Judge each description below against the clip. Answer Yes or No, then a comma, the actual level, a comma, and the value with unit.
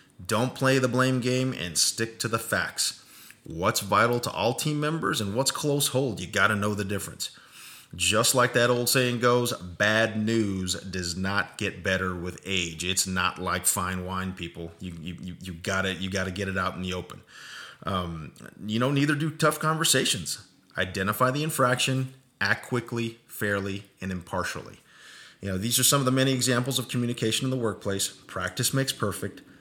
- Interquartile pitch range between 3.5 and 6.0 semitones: Yes, wide, 5.4 semitones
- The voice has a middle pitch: No, low, 105 Hz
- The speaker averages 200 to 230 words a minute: No, average, 185 wpm